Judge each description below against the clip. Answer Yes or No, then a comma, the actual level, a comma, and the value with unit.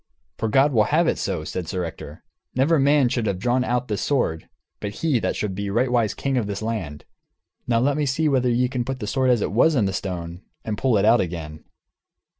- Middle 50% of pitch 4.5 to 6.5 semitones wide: Yes, average, 4.9 semitones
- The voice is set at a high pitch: No, low, 120 Hz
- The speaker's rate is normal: No, fast, 225 wpm